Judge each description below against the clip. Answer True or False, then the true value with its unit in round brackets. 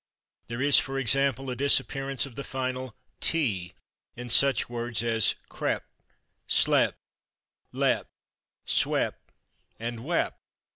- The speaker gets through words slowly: True (110 wpm)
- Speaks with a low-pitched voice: True (130 Hz)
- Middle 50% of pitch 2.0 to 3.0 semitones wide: True (2.7 semitones)